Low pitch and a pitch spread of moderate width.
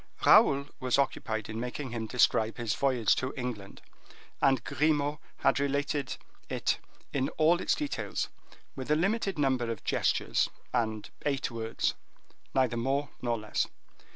Yes: low, 130 Hz; average, 3.6 semitones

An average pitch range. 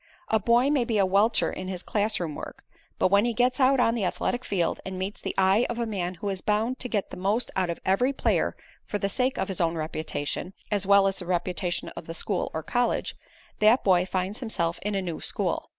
Yes: average, 4.0 semitones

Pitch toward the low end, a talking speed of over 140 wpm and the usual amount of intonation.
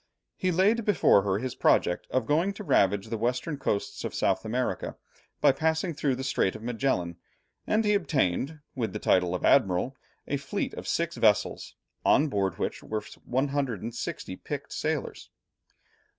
No: low, 130 Hz; average, 165 wpm; wide, 7.1 semitones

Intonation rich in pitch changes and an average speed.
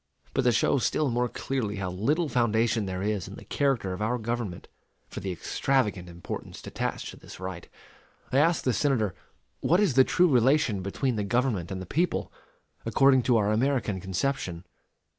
Yes: wide, 5.7 semitones; average, 180 wpm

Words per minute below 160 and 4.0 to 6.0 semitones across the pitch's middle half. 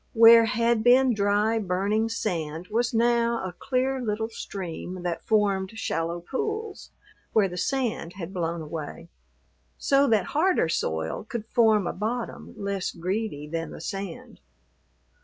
Yes: average, 140 wpm; average, 4.7 semitones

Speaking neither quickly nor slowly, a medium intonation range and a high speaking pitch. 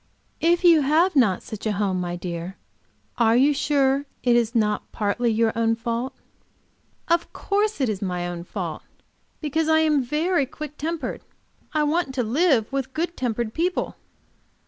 No: average, 165 wpm; wide, 6.0 semitones; very high, 265 Hz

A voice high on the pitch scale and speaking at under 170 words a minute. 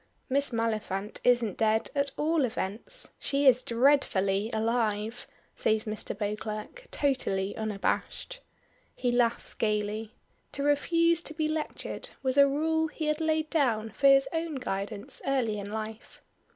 Yes: high, 245 Hz; average, 140 wpm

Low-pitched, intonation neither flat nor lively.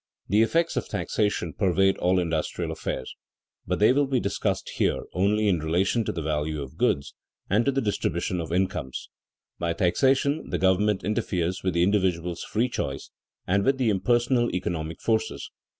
Yes: very low, 95 Hz; average, 4.5 semitones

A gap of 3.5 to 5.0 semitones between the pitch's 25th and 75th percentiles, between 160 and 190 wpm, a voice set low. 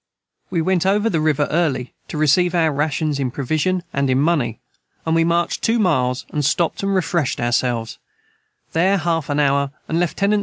No: average, 3.8 semitones; average, 180 wpm; medium, 155 Hz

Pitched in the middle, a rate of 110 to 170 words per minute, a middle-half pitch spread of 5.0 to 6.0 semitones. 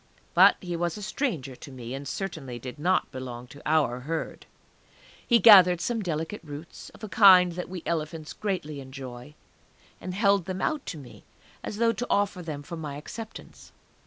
No: medium, 165 Hz; average, 180 wpm; wide, 5.4 semitones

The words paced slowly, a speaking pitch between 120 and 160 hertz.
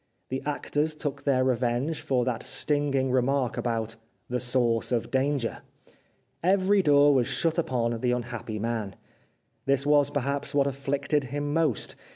No: average, 155 wpm; low, 135 Hz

